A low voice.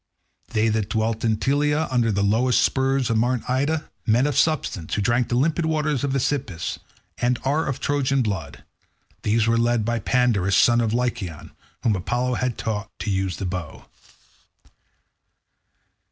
Yes: low, 120 Hz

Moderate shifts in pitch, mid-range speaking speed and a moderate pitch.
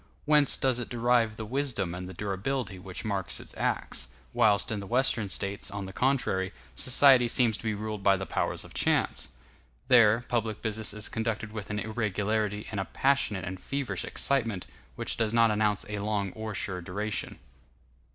No: average, 3.0 semitones; average, 180 wpm; low, 110 Hz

